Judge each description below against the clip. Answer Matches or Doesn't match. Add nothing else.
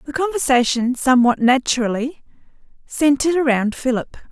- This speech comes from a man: Doesn't match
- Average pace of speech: Doesn't match